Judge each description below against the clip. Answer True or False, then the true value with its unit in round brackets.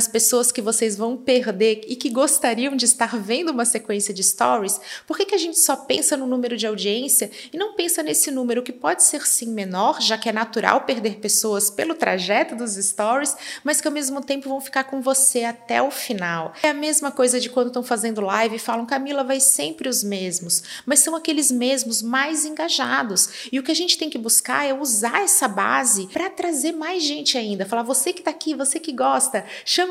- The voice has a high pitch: True (255 Hz)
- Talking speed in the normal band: False (215 wpm)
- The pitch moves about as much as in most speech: True (4.6 semitones)